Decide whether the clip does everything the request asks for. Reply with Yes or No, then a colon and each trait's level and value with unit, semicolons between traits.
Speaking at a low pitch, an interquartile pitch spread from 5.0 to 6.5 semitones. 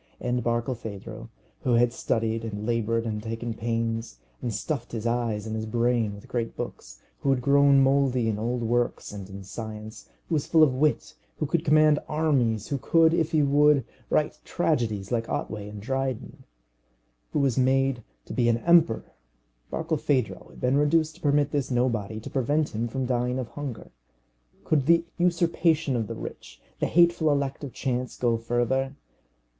No: low, 125 Hz; average, 3.9 semitones